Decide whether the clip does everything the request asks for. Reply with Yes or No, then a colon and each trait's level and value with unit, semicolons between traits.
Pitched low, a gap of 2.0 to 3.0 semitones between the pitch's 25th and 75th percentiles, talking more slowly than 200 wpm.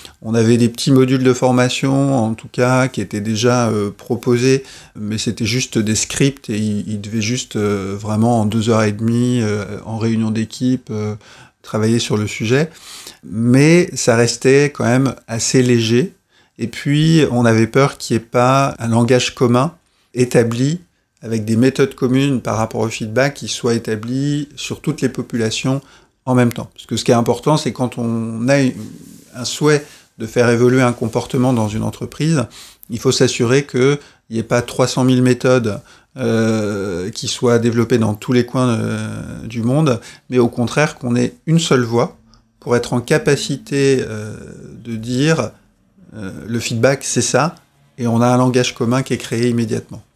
Yes: low, 120 Hz; average, 2.7 semitones; average, 180 wpm